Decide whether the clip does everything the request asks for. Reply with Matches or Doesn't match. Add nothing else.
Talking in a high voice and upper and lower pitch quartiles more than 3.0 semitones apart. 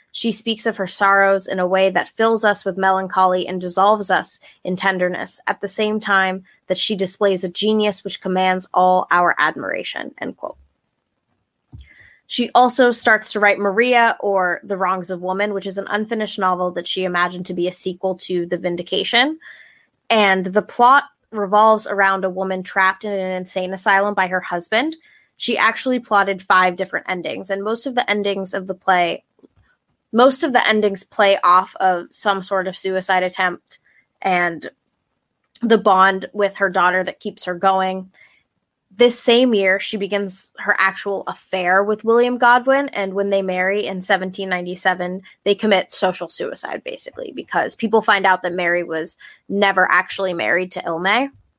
Doesn't match